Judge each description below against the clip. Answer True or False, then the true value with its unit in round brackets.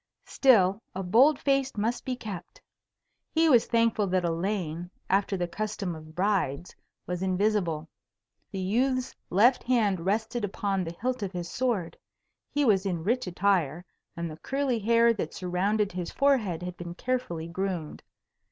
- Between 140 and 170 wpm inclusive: True (150 wpm)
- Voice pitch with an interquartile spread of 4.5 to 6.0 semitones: True (4.8 semitones)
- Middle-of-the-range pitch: False (195 Hz)